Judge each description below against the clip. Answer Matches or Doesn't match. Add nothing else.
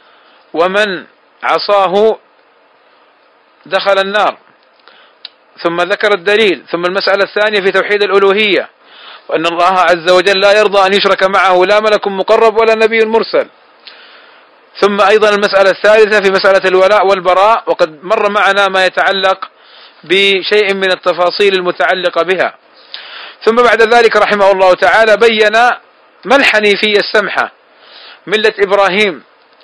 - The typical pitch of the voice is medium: Doesn't match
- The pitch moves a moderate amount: Doesn't match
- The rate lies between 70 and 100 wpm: Doesn't match